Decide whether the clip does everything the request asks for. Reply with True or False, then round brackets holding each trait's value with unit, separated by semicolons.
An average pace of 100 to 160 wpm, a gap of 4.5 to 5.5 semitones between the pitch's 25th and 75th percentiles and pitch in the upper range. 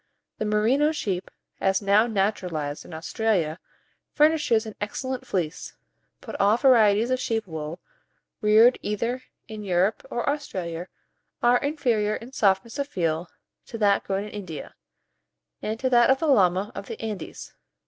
False (150 wpm; 4.1 semitones; 210 Hz)